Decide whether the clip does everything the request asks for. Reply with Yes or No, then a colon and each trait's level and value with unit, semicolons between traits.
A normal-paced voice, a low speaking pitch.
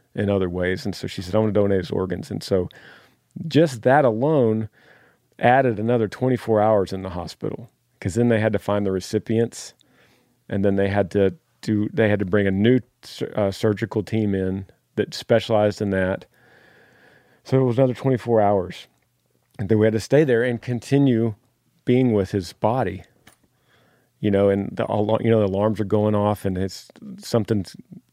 Yes: average, 180 wpm; low, 110 Hz